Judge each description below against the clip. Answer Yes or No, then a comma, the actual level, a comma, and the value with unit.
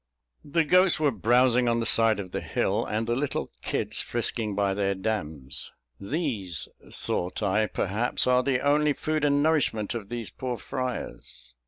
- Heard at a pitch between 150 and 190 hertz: No, low, 120 Hz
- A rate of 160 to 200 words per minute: Yes, average, 165 wpm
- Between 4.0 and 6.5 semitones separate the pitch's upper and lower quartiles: Yes, wide, 5.5 semitones